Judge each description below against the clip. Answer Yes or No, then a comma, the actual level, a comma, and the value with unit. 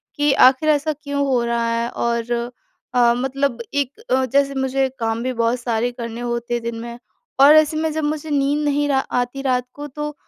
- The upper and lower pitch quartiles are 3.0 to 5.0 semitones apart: Yes, average, 3.4 semitones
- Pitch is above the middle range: Yes, very high, 265 Hz